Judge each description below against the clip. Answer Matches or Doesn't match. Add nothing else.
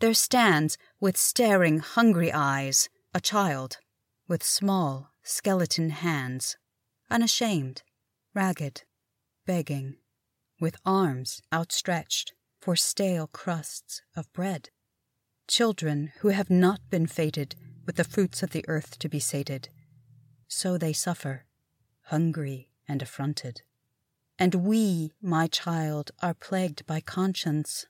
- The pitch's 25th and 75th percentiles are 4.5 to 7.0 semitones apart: Matches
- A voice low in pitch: Doesn't match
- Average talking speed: Doesn't match